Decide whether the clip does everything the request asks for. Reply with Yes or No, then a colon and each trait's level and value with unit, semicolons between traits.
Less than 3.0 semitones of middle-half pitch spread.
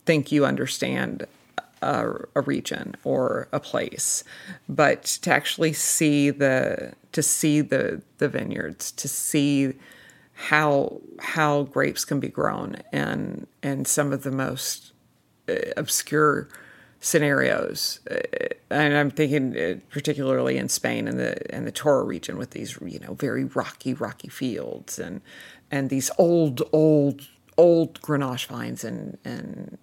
Yes: narrow, 2.5 semitones